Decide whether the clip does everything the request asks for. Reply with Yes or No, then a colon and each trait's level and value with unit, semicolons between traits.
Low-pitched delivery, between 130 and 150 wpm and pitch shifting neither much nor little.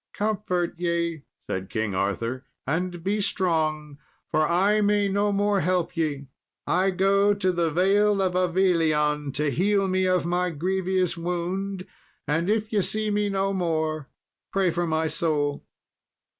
No: medium, 180 Hz; average, 145 wpm; average, 3.7 semitones